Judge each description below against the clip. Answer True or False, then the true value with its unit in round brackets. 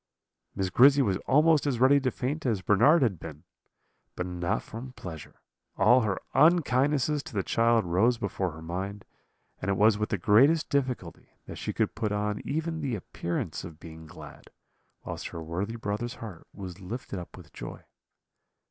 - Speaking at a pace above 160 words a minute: True (175 wpm)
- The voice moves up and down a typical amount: False (6.0 semitones)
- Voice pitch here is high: False (105 Hz)